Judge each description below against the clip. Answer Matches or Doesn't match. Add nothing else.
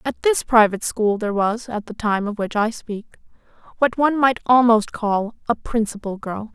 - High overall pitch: Matches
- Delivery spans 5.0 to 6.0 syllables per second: Matches